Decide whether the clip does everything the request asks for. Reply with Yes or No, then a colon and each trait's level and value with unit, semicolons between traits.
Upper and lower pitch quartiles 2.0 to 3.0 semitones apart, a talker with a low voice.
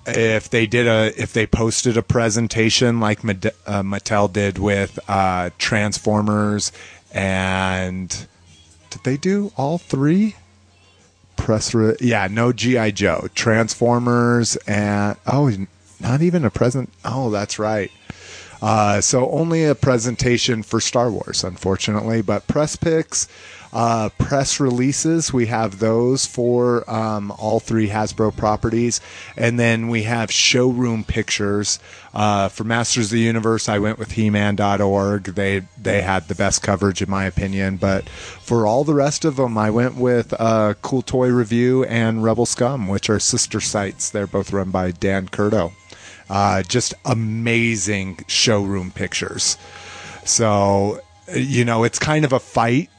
No: average, 3.4 semitones; low, 110 Hz